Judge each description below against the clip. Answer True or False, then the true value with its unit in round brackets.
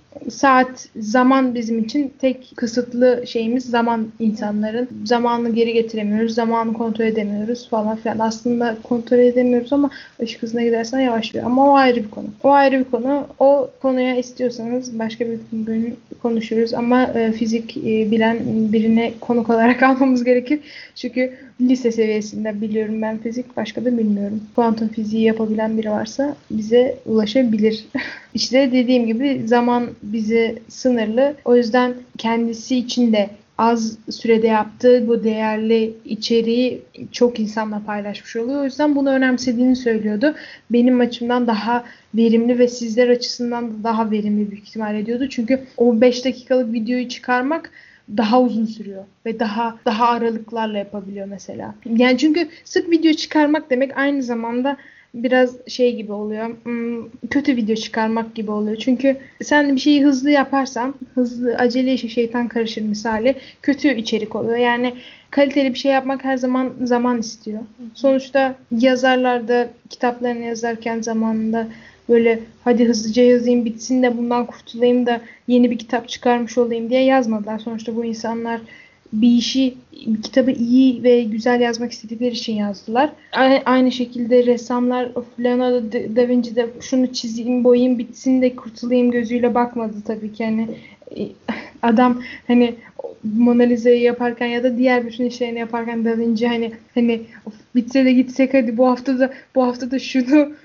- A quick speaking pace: True (145 wpm)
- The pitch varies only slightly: True (1.9 semitones)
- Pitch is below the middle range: False (240 Hz)